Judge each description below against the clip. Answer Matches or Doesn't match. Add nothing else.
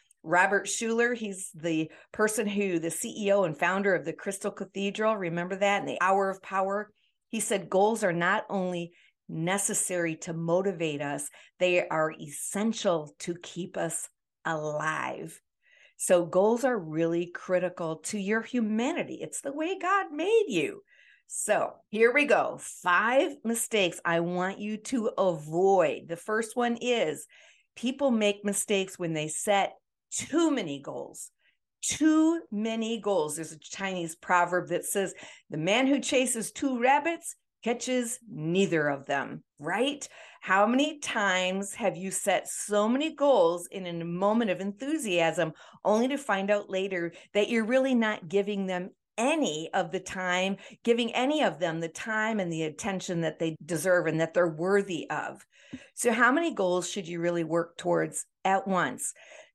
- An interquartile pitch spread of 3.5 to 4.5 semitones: Doesn't match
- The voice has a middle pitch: Doesn't match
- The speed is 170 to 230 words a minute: Doesn't match